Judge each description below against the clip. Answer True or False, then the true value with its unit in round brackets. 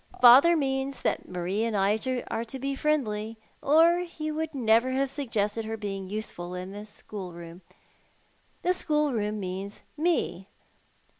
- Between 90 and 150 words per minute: True (140 wpm)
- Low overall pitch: False (225 Hz)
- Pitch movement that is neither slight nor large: False (5.8 semitones)